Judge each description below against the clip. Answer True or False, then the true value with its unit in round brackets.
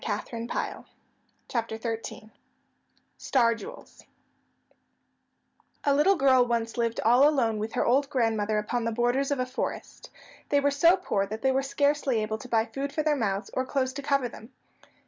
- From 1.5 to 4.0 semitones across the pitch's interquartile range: True (3.7 semitones)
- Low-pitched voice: False (245 Hz)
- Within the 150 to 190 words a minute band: True (165 wpm)